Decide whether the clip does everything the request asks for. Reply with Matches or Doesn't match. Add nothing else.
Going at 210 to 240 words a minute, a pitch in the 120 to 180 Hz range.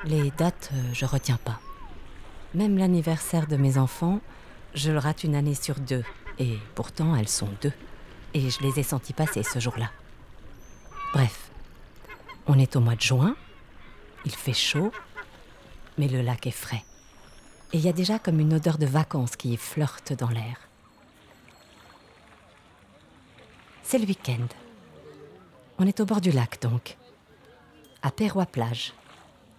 Doesn't match